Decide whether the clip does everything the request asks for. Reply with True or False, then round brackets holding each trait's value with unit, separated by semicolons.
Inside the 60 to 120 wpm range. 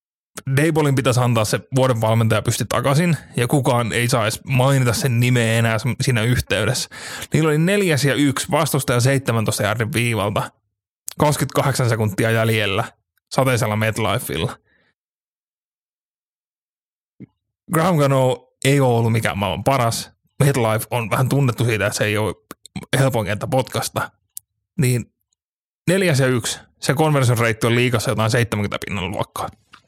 False (130 wpm)